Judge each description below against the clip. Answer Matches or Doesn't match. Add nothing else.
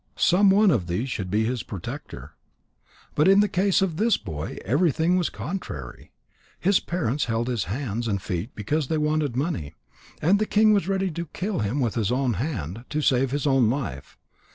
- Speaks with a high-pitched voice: Doesn't match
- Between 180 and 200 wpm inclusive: Matches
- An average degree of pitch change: Doesn't match